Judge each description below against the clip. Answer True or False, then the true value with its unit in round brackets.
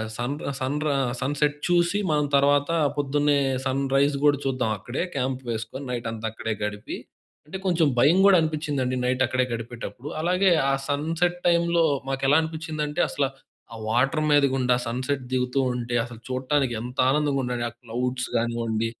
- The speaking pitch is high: False (135 Hz)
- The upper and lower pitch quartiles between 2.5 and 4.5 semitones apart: True (3.2 semitones)